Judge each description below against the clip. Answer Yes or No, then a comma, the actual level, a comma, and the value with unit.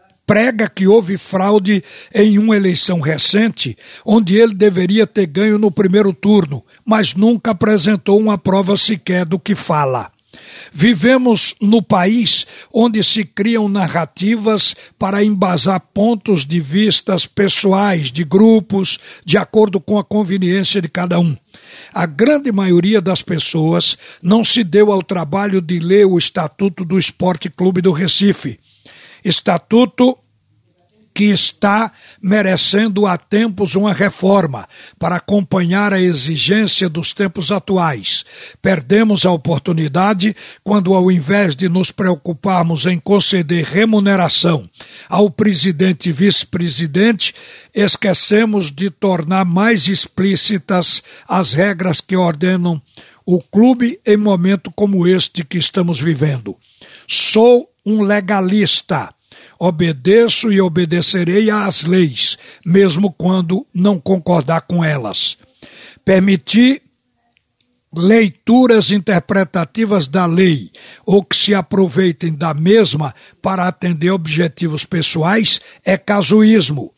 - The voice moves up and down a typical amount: Yes, average, 3.0 semitones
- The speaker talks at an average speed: No, slow, 115 wpm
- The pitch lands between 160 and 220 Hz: Yes, high, 190 Hz